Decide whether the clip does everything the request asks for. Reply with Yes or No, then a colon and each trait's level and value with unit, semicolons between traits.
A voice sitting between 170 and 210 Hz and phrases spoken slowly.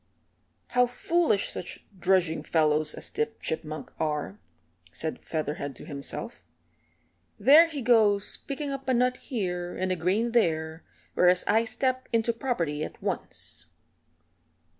Yes: high, 190 Hz; slow, 130 wpm